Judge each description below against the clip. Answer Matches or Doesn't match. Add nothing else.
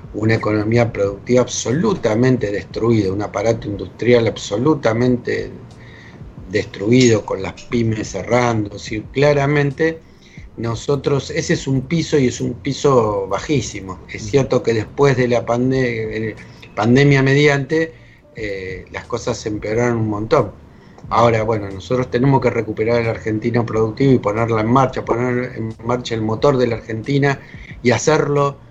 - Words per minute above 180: Doesn't match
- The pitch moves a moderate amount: Matches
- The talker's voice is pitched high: Doesn't match